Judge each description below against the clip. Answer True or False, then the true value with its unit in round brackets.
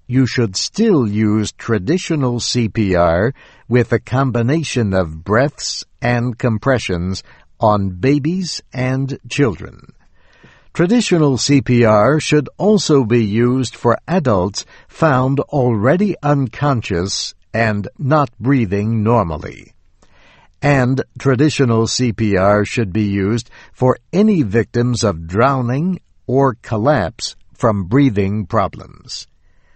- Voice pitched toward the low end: True (120 Hz)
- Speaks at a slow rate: True (95 wpm)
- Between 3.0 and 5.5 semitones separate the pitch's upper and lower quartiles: True (4.4 semitones)